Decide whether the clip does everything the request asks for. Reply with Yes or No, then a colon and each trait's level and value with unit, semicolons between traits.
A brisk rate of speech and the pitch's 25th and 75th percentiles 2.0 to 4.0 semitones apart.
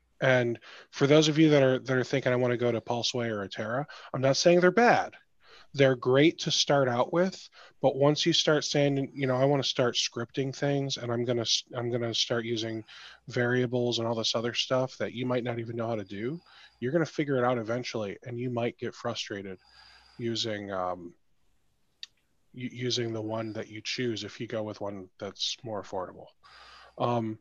Yes: fast, 210 wpm; average, 2.7 semitones